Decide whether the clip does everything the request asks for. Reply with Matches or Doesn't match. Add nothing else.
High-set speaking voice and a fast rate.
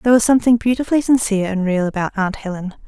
Matches